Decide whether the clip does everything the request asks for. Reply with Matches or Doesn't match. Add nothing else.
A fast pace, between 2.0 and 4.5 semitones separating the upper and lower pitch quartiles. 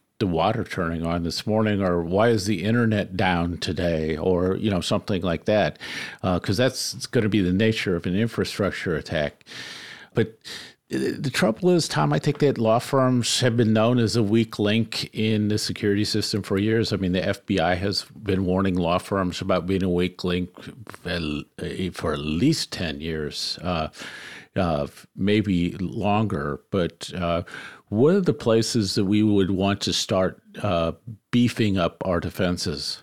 Doesn't match